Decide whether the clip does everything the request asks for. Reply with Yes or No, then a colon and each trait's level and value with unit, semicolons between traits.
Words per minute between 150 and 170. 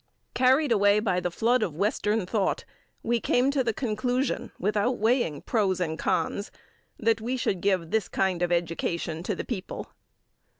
Yes: average, 165 wpm